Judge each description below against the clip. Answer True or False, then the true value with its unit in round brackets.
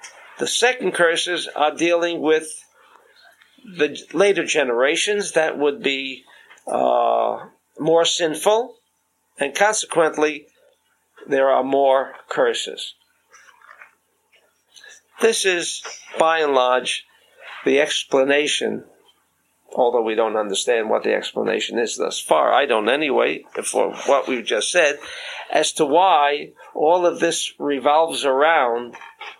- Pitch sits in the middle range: True (165 Hz)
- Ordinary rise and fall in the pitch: False (7.8 semitones)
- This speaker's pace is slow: True (110 wpm)